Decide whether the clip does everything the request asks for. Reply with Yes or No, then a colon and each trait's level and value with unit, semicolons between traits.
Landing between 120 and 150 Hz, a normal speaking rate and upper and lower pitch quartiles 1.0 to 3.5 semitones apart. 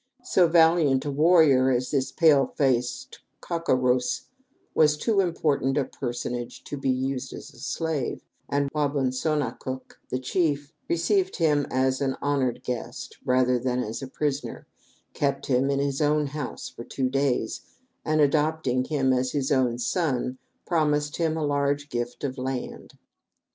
Yes: medium, 140 Hz; average, 165 wpm; average, 2.8 semitones